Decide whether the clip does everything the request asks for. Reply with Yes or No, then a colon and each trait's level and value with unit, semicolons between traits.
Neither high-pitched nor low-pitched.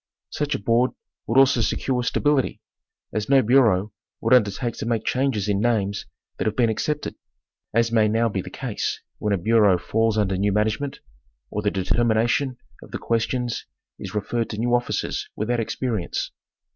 No: low, 115 Hz